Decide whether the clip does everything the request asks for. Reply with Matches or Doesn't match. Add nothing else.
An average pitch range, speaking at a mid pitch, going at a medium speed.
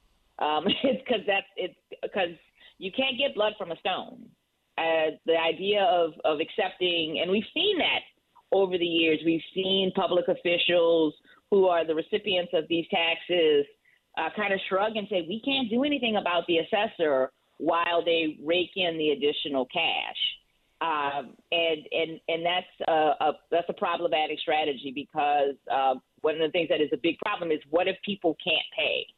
Matches